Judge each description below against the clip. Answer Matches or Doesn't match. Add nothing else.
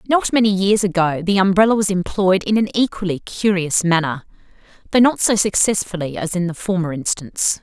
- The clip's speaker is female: Matches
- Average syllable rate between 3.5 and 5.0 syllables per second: Doesn't match